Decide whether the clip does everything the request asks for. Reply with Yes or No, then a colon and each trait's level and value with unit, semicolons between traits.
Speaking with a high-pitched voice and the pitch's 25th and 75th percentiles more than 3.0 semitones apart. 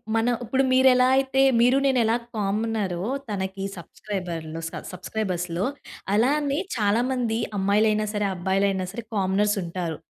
Yes: high, 205 Hz; average, 3.7 semitones